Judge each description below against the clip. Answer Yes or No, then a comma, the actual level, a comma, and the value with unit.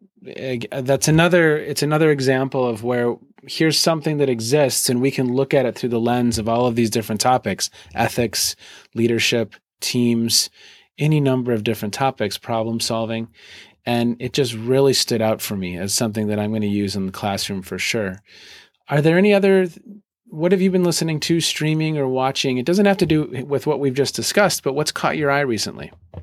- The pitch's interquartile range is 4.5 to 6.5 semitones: Yes, average, 4.9 semitones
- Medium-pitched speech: No, low, 130 Hz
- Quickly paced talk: No, average, 195 wpm